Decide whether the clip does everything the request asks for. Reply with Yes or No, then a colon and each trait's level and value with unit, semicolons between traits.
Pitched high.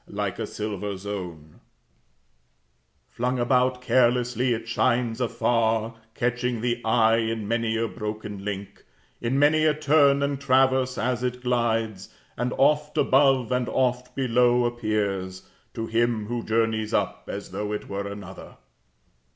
No: low, 120 Hz